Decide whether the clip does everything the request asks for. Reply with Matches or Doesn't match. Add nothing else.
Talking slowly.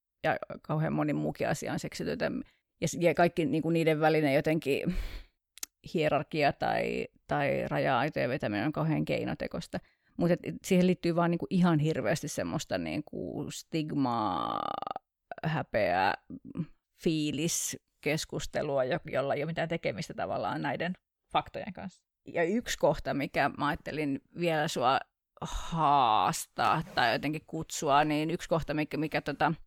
Doesn't match